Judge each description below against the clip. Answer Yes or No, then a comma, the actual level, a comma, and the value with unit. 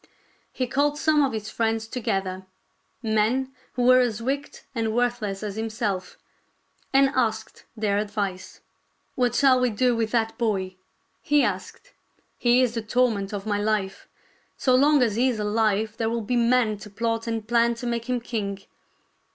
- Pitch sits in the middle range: No, high, 225 Hz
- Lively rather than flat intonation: No, average, 2.9 semitones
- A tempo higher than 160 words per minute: Yes, average, 185 wpm